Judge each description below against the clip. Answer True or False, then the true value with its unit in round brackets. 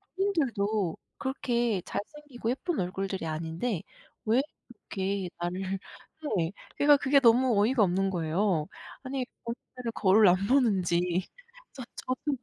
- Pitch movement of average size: False (5.8 semitones)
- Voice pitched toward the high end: True (210 Hz)